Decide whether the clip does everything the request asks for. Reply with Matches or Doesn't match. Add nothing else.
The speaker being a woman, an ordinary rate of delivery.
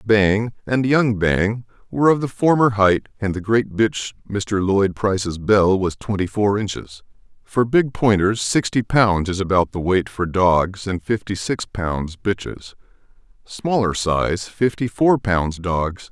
Doesn't match